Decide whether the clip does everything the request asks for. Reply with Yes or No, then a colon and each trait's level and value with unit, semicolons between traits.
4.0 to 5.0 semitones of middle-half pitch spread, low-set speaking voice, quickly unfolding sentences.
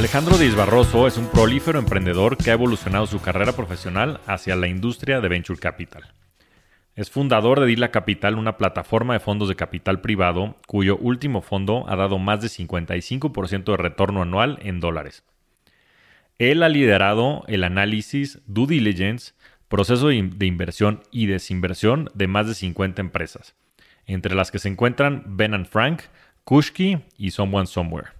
No: average, 4.3 semitones; low, 105 Hz; average, 155 wpm